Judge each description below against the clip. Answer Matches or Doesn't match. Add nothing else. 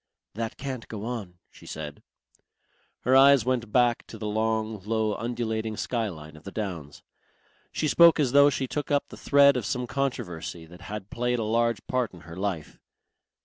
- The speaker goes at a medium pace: Matches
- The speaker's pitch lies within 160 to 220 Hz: Doesn't match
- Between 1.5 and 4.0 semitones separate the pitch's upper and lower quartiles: Doesn't match